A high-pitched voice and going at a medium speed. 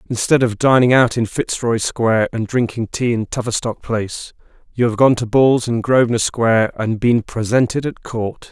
No: low, 115 Hz; average, 185 wpm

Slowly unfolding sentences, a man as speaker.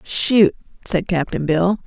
No: slow, 130 wpm; female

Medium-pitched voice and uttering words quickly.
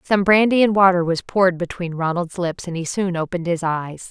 Yes: medium, 180 Hz; fast, 220 wpm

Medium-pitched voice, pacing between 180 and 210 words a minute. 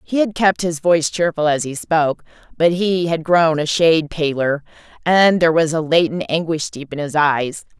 Yes: medium, 160 Hz; average, 200 wpm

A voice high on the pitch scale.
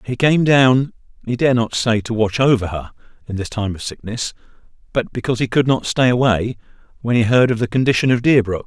No: low, 115 Hz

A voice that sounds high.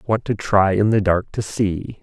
No: low, 100 Hz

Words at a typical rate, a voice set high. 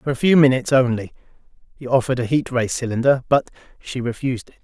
No: average, 195 wpm; low, 125 Hz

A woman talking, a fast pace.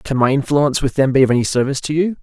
No: male; fast, 295 wpm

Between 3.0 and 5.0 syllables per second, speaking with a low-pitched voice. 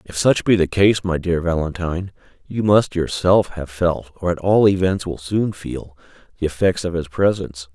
Yes: 4.8 syllables/s; very low, 90 Hz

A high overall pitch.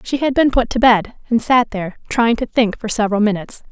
Yes: high, 225 Hz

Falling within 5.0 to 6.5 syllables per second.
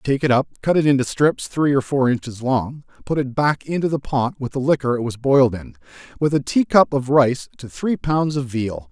Yes: 5.2 syllables/s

